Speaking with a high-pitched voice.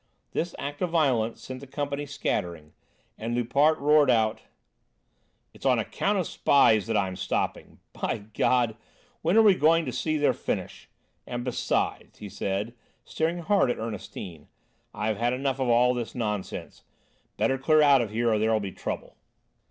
No: low, 125 Hz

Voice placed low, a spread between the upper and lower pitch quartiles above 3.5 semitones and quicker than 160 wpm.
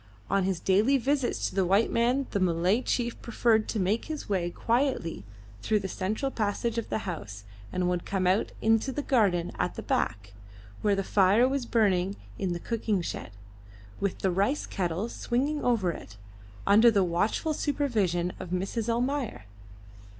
No: high, 205 Hz; average, 4.6 semitones; average, 170 wpm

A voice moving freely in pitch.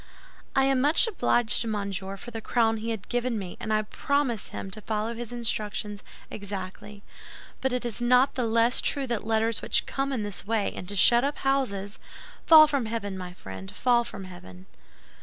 No: average, 3.5 semitones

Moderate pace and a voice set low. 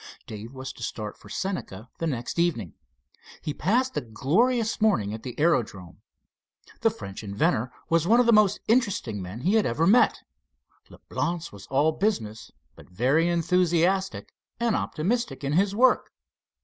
No: average, 155 wpm; medium, 165 Hz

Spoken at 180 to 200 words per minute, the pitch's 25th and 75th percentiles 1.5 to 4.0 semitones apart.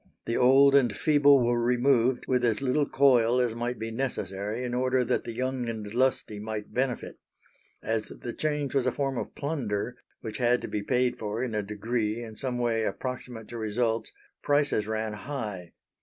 Yes: average, 185 wpm; average, 2.9 semitones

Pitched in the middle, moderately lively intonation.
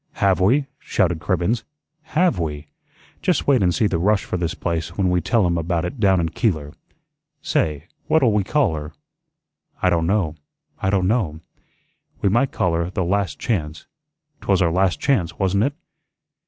No: very low, 90 Hz; average, 4.2 semitones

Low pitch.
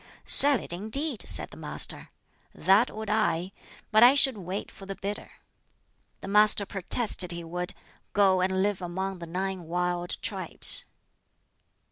No: high, 195 Hz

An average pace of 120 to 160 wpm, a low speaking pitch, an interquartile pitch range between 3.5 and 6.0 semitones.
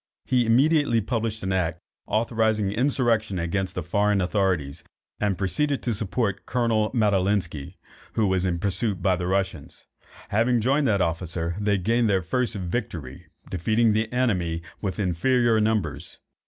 Yes: average, 140 wpm; low, 105 Hz; average, 4.1 semitones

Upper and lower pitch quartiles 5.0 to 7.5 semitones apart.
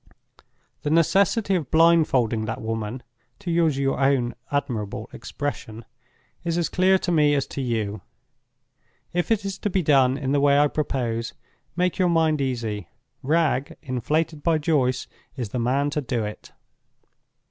Yes: average, 5.3 semitones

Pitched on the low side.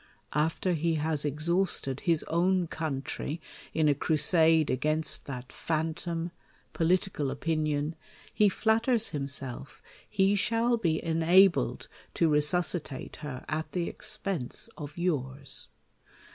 No: medium, 160 Hz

